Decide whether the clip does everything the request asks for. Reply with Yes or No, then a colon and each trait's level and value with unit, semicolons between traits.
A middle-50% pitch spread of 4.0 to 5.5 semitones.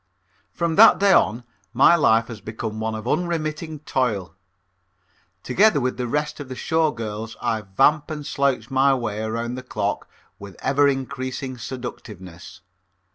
Yes: average, 5.1 semitones